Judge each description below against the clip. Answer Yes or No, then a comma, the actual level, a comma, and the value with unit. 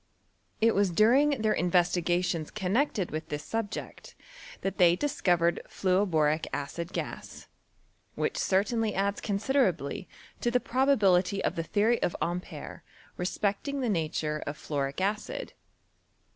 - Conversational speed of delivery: No, slow, 130 wpm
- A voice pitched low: No, high, 190 Hz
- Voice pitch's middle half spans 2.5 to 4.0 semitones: No, average, 4.5 semitones